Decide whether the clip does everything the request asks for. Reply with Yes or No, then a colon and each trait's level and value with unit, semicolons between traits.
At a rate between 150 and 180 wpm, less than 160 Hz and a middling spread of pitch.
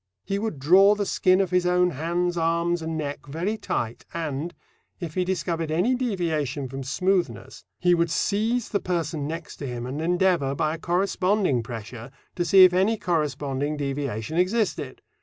No: average, 170 wpm; medium, 170 Hz; average, 4.2 semitones